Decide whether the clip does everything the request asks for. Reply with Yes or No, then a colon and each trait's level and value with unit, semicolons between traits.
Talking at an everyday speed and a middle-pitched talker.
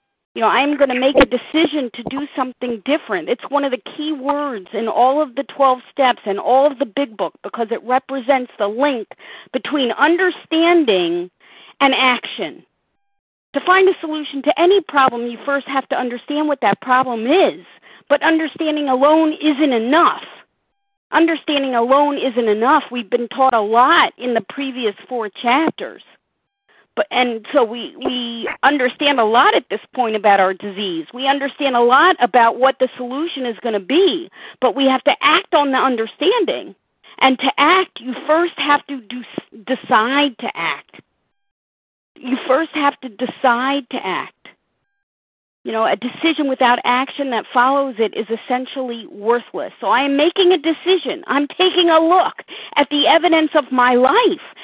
No: average, 170 wpm; very high, 270 Hz